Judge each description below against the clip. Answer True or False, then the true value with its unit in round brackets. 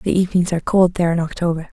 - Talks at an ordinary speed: False (235 wpm)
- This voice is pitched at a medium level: True (175 Hz)